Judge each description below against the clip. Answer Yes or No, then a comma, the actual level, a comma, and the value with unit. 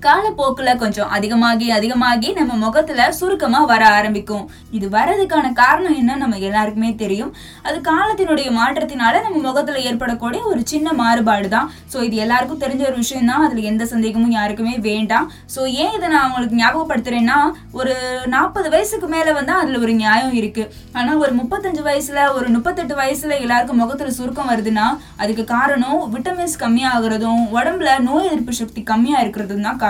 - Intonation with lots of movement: No, average, 4.4 semitones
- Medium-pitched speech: No, very high, 250 Hz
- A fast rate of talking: Yes, fast, 150 wpm